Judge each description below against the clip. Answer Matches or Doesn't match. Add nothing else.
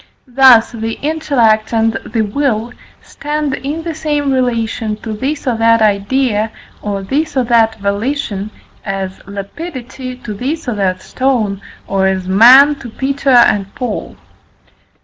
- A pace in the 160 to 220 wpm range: Doesn't match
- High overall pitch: Matches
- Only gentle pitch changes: Doesn't match